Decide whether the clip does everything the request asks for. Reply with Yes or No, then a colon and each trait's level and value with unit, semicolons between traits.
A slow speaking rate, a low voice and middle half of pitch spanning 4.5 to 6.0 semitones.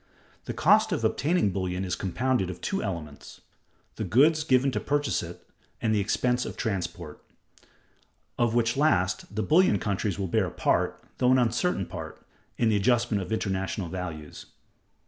No: average, 165 wpm; low, 110 Hz; wide, 5.5 semitones